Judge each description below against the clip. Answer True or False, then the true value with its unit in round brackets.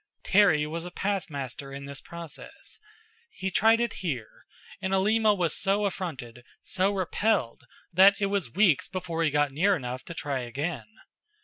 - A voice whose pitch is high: False (170 Hz)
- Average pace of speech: True (165 wpm)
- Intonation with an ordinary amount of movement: False (5.8 semitones)